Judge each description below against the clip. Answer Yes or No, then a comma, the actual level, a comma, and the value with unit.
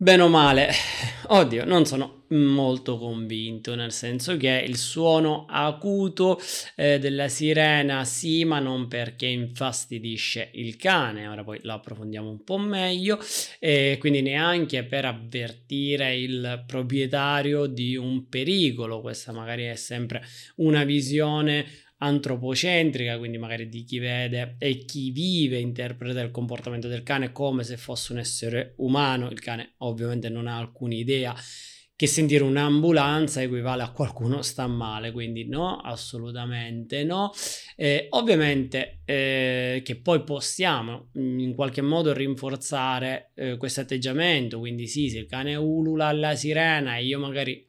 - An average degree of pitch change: Yes, average, 3.3 semitones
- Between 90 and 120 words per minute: No, average, 140 wpm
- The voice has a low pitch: Yes, low, 130 Hz